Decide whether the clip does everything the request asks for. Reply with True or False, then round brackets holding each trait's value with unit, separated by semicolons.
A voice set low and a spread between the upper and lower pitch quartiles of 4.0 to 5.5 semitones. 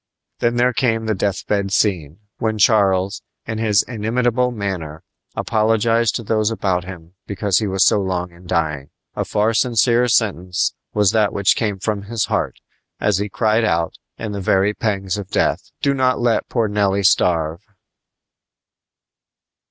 False (105 Hz; 3.0 semitones)